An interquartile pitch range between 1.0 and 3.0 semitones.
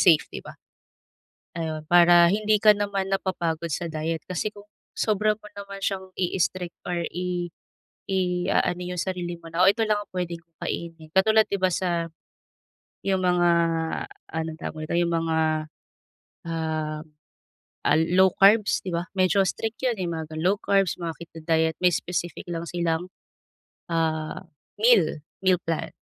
Yes: average, 2.7 semitones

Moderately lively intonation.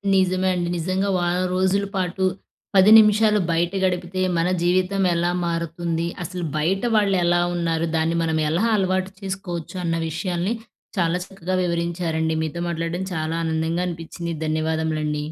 No: narrow, 2.2 semitones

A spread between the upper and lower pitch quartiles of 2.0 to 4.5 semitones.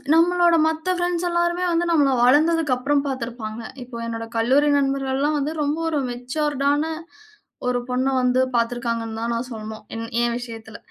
No: average, 4.9 semitones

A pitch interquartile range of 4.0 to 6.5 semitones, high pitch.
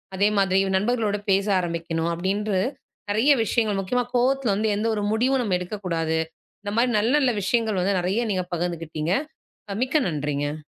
Yes: average, 4.3 semitones; high, 200 Hz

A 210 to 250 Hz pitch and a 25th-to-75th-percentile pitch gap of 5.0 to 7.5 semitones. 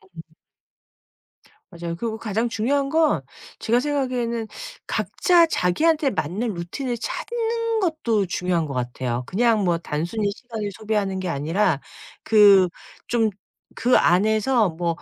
Yes: high, 215 Hz; wide, 6.1 semitones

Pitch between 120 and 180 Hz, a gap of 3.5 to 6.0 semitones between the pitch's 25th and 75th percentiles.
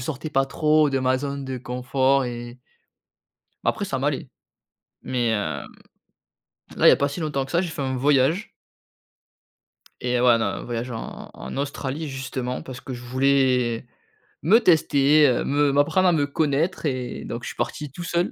No: low, 135 Hz; average, 2.9 semitones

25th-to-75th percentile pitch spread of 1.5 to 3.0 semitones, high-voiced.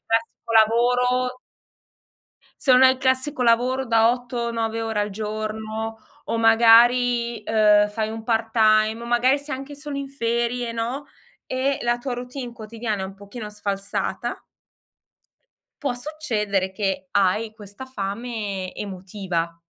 Yes: average, 2.7 semitones; high, 230 Hz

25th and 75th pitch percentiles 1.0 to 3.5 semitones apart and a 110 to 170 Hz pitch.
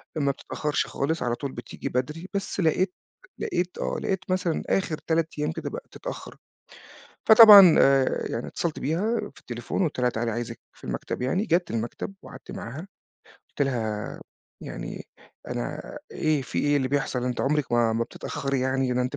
No: average, 5.0 semitones; medium, 140 Hz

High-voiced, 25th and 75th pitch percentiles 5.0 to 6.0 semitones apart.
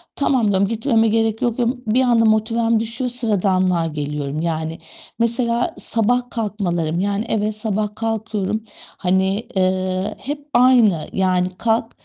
No: high, 215 Hz; average, 3.7 semitones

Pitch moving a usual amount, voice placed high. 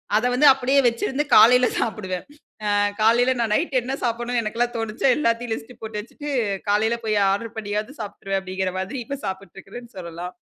Yes: average, 3.1 semitones; high, 225 Hz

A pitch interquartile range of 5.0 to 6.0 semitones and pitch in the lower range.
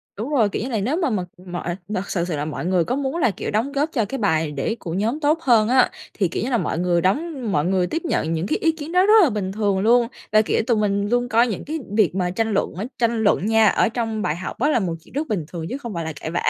No: wide, 5.5 semitones; high, 215 Hz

